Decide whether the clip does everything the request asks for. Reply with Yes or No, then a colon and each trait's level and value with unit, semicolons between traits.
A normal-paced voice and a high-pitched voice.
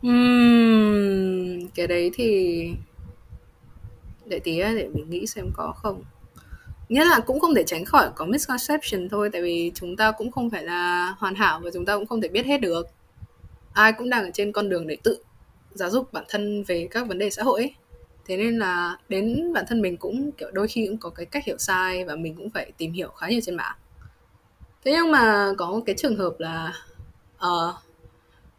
Yes: average, 205 wpm; high, 200 Hz